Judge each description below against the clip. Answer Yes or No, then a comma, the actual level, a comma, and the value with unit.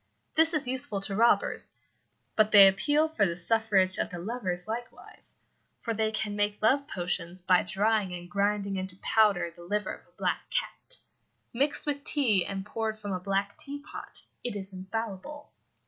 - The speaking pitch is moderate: No, high, 205 Hz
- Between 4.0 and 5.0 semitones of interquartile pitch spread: No, average, 3.6 semitones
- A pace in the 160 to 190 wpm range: Yes, average, 170 wpm